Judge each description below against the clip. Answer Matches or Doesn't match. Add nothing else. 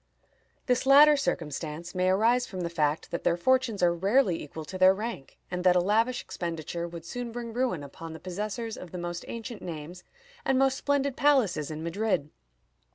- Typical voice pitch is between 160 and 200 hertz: Matches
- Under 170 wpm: Doesn't match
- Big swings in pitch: Matches